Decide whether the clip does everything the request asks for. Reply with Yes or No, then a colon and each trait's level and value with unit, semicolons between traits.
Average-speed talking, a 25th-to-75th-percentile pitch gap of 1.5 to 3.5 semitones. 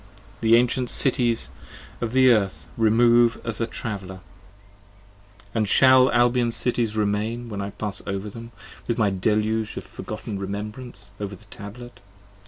Yes: average, 145 wpm; average, 2.8 semitones